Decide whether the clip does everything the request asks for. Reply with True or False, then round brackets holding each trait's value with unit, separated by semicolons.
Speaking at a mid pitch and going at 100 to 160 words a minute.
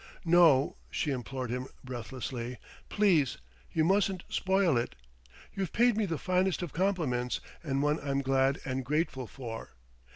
True (145 Hz; 140 wpm)